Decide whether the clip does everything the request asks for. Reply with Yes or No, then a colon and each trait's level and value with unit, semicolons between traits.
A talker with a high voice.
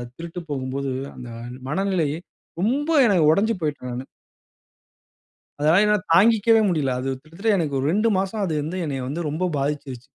No: medium, 165 Hz